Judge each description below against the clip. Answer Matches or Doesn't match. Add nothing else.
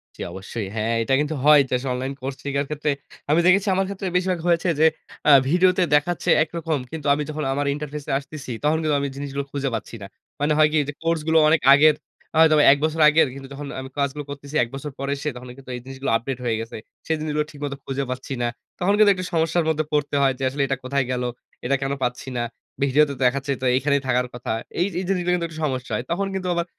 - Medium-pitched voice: Matches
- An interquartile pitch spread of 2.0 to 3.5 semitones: Matches